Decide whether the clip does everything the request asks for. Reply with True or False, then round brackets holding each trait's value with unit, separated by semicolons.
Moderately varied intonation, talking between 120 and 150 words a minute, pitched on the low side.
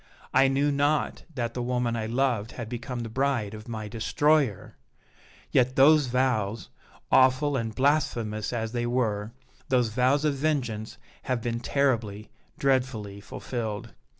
True (3.4 semitones; 140 wpm; 120 Hz)